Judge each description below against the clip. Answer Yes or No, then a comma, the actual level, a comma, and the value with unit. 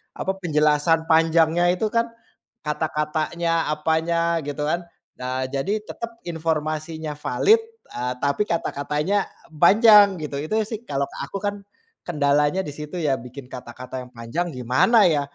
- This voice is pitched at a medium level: Yes, medium, 160 Hz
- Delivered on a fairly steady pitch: No, average, 3.7 semitones